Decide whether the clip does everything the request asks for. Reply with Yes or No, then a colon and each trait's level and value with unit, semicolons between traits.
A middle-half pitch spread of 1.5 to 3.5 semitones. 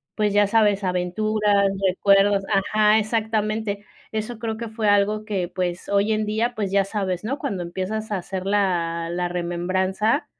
Yes: narrow, 2.5 semitones